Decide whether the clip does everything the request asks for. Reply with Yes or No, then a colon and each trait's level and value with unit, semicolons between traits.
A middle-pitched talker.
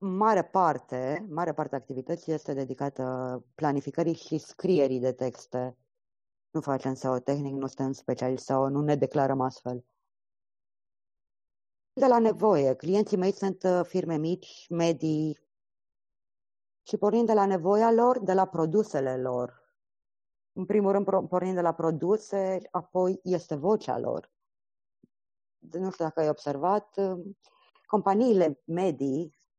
Yes: medium, 160 Hz